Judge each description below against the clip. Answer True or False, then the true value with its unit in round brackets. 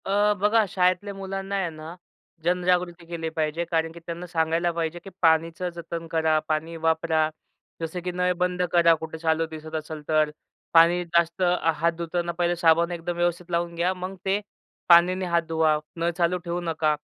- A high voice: False (170 Hz)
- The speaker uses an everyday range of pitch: False (1.7 semitones)